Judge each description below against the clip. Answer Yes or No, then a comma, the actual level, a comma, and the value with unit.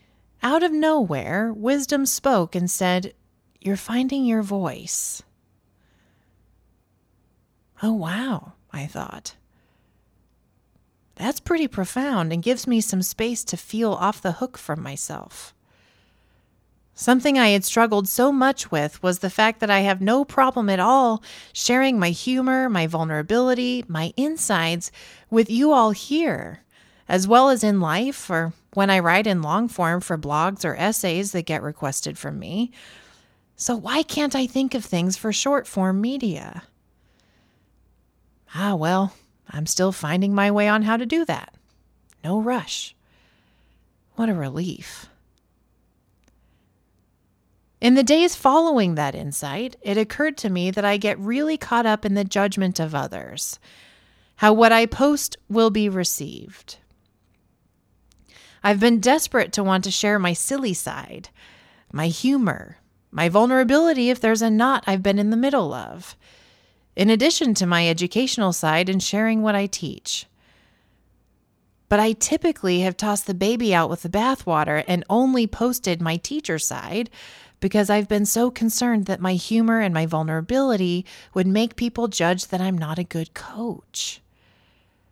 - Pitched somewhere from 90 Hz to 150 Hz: No, high, 200 Hz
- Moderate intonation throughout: No, wide, 6.5 semitones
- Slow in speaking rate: No, average, 145 wpm